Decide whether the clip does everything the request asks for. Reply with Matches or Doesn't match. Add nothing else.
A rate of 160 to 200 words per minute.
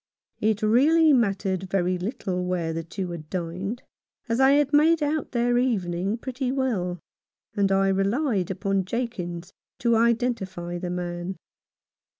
Doesn't match